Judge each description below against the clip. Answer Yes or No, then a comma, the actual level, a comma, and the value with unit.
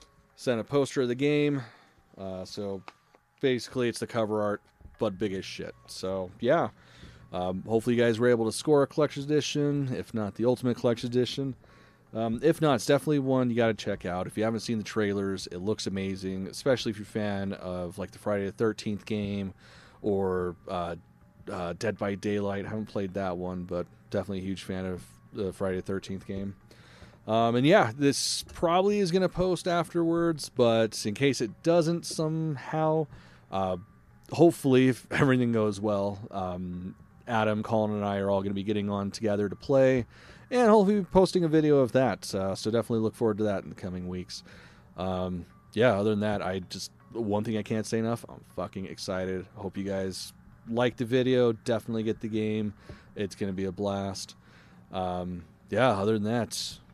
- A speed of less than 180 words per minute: No, average, 190 wpm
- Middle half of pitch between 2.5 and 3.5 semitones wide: No, average, 4.4 semitones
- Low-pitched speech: Yes, low, 110 Hz